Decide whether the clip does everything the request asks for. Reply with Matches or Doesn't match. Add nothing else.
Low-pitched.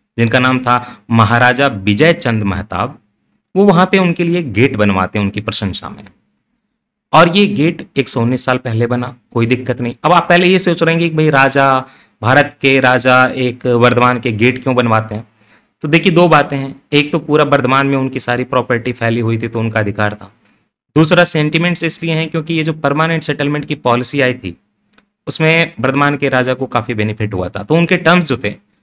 Matches